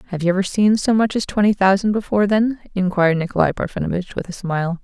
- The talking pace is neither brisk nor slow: No, fast, 210 wpm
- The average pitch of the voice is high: Yes, high, 195 Hz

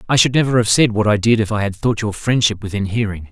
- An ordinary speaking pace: No, fast, 290 wpm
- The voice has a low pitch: Yes, low, 110 Hz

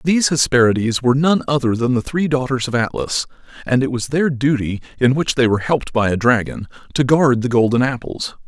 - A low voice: Yes, low, 130 Hz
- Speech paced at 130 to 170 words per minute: No, fast, 205 wpm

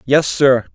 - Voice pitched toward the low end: Yes, low, 120 Hz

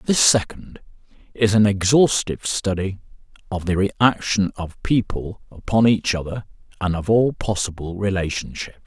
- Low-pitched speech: Yes, low, 100 Hz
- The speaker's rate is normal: No, slow, 130 wpm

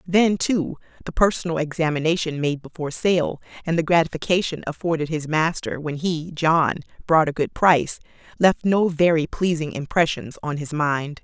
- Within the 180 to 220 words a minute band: No, average, 150 wpm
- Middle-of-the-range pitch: Yes, medium, 160 Hz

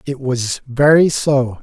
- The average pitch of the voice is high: No, low, 135 Hz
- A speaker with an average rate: Yes, average, 150 wpm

